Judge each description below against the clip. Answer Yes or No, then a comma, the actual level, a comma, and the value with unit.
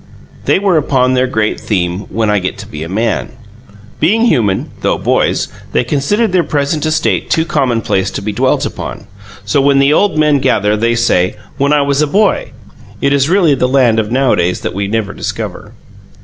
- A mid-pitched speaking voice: No, low, 130 Hz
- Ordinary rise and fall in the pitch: No, wide, 5.9 semitones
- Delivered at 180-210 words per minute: Yes, average, 190 wpm